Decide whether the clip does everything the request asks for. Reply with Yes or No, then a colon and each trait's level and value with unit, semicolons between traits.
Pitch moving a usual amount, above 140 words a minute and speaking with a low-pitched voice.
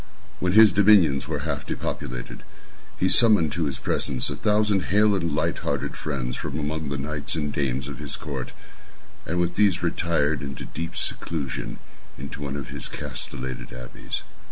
Yes: average, 4.7 semitones; average, 170 wpm; very low, 75 Hz